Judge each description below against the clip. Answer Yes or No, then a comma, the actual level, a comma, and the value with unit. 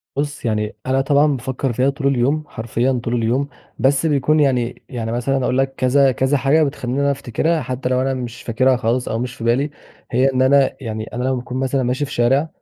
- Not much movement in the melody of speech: Yes, narrow, 2.3 semitones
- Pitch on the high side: No, low, 130 Hz